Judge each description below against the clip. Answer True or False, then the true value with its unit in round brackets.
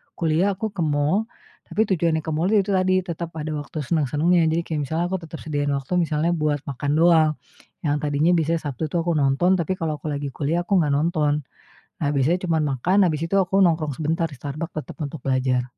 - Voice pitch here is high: False (160 Hz)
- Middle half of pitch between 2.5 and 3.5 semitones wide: True (2.9 semitones)